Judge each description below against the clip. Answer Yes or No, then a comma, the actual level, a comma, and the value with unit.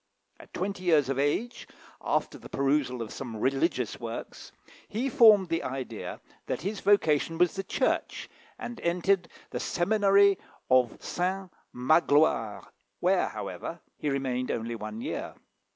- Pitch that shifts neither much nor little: No, wide, 7.2 semitones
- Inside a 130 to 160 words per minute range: Yes, slow, 135 wpm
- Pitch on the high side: No, medium, 155 Hz